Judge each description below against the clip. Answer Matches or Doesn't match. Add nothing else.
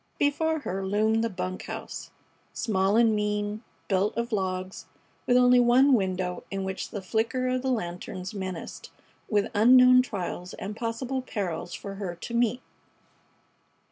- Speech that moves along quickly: Doesn't match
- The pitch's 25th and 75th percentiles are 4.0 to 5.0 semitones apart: Matches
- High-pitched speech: Matches